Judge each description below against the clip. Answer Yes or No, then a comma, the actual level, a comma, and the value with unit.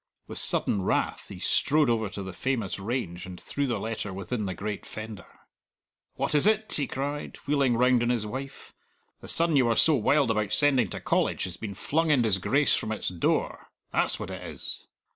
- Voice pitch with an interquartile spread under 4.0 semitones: No, wide, 5.4 semitones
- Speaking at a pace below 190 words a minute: No, average, 200 wpm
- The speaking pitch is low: Yes, low, 120 Hz